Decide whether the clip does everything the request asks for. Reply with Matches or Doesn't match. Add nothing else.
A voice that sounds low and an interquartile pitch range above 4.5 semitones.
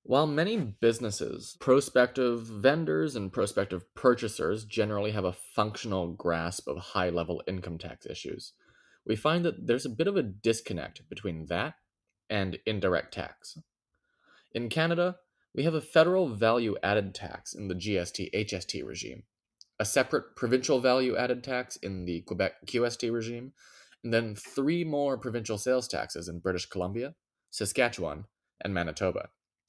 Matches